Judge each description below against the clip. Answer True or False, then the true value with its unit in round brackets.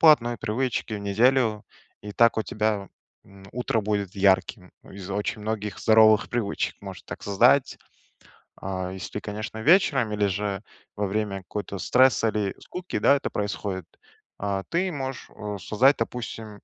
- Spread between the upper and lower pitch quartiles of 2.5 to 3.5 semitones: True (3.1 semitones)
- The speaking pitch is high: False (105 Hz)